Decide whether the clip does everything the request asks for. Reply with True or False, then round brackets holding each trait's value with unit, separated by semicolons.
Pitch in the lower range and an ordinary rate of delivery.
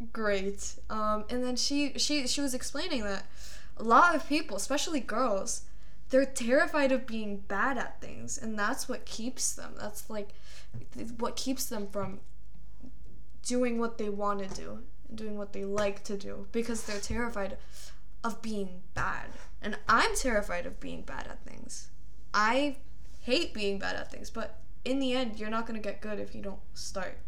False (225 Hz; 180 wpm)